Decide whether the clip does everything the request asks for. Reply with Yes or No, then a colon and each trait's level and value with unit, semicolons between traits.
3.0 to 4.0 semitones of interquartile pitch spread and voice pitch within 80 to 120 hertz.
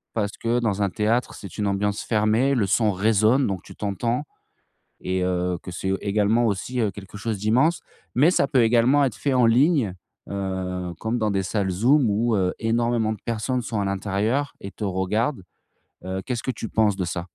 Yes: average, 3.5 semitones; low, 110 Hz